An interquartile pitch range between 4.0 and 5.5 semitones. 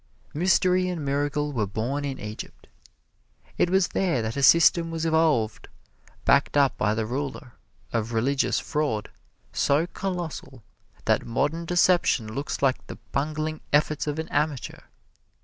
Yes: average, 4.4 semitones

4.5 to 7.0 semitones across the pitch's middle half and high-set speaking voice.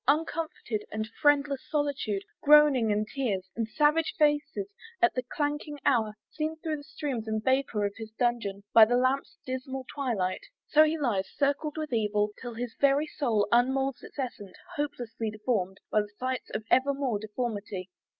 Yes: average, 5.1 semitones; very high, 255 Hz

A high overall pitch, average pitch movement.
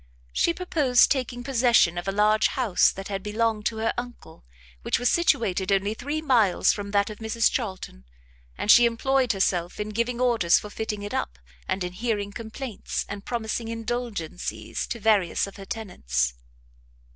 Yes: high, 220 Hz; average, 3.5 semitones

